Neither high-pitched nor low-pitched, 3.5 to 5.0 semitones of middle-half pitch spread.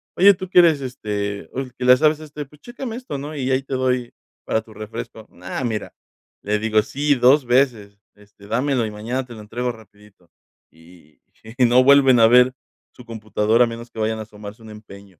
No: low, 120 Hz; average, 3.9 semitones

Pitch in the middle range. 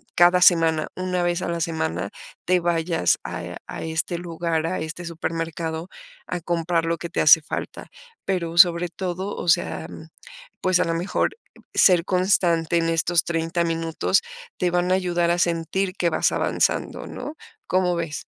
Yes: medium, 170 Hz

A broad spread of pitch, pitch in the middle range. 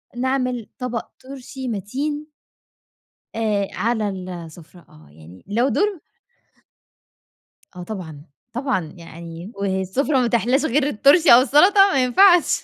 No: wide, 6.7 semitones; high, 235 Hz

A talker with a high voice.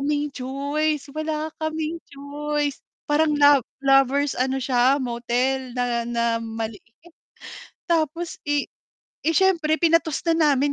Yes: very high, 285 Hz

